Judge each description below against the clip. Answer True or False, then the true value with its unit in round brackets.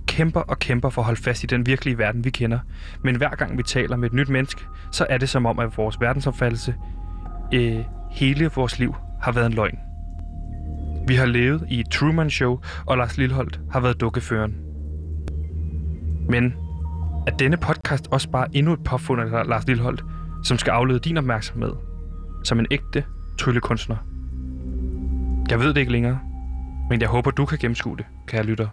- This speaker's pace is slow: False (180 wpm)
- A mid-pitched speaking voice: False (115 Hz)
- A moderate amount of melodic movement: False (8.5 semitones)